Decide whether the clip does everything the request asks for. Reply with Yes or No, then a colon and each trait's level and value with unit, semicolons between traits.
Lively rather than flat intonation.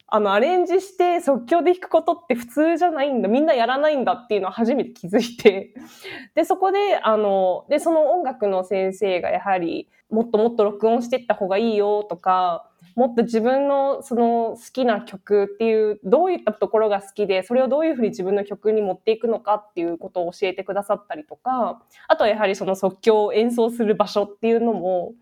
No: average, 4.8 semitones